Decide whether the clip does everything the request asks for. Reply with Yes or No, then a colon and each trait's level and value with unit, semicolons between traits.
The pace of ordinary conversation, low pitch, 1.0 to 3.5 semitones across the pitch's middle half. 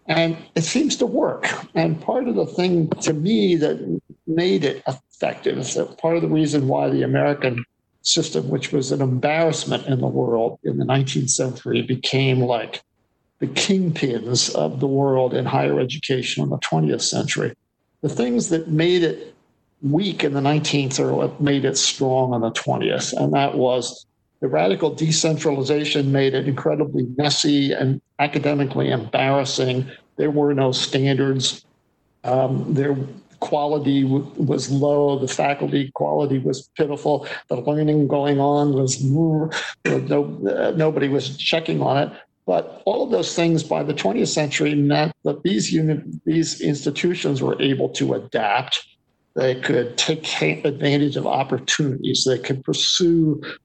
No: average, 150 wpm; medium, 145 Hz; average, 3.1 semitones